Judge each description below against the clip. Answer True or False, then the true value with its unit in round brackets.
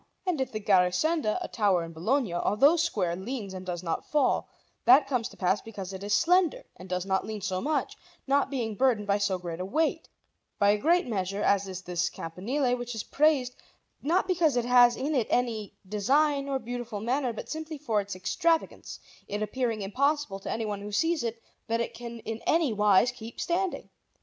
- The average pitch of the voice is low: False (230 Hz)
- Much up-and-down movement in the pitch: True (5.8 semitones)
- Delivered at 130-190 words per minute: False (200 wpm)